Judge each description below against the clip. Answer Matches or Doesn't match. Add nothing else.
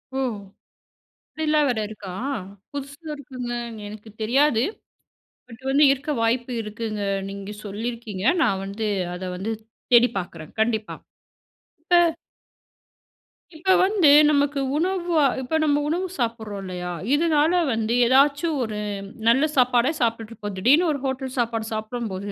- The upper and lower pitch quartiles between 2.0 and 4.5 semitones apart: Doesn't match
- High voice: Matches